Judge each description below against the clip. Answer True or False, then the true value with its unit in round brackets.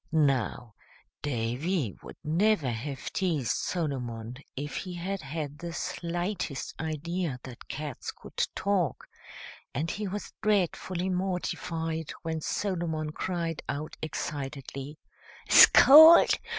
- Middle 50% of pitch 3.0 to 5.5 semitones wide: True (4.5 semitones)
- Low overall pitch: False (160 Hz)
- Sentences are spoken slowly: True (105 wpm)